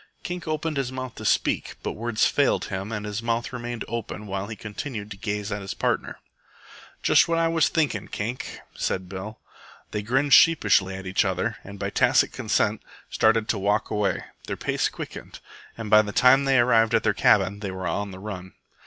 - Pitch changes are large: No, average, 3.5 semitones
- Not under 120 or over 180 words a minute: No, average, 195 wpm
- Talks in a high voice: No, low, 110 Hz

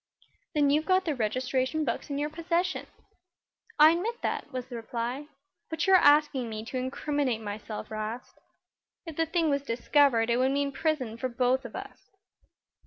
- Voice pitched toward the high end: Yes, very high, 280 Hz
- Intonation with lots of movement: No, average, 4.6 semitones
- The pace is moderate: Yes, average, 170 wpm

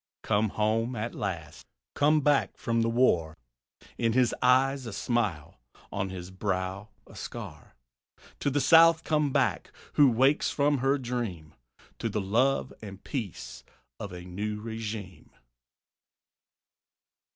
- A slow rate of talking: Yes, slow, 130 wpm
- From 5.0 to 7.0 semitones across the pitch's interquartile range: Yes, wide, 5.5 semitones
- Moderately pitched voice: No, low, 115 Hz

